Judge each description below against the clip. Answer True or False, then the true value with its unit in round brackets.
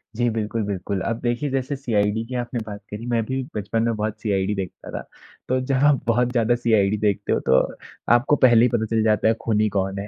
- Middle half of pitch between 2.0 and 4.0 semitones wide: True (2.6 semitones)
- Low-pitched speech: True (110 Hz)